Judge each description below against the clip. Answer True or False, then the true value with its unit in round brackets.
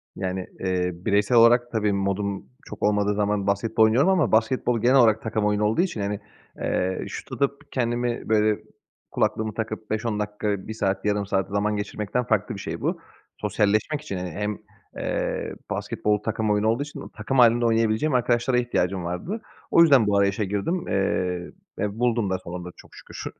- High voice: False (105 Hz)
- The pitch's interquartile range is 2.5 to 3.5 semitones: True (3.0 semitones)